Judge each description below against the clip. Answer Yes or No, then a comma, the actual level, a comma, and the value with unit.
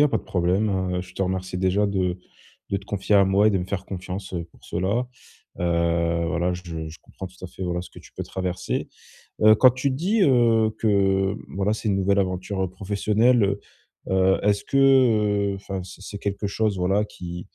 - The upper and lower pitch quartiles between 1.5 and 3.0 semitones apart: Yes, narrow, 2.4 semitones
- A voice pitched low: Yes, very low, 95 Hz